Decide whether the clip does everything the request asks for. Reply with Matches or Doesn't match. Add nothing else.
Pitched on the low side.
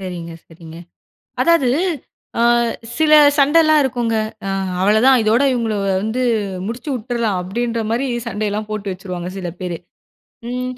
Doesn't match